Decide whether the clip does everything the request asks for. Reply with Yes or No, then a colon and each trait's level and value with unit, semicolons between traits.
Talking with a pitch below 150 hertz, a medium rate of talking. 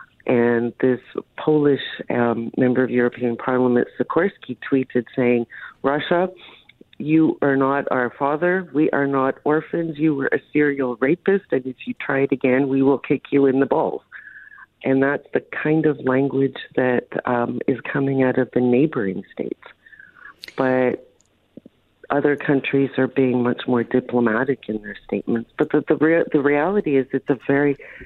Yes: low, 135 Hz; average, 160 wpm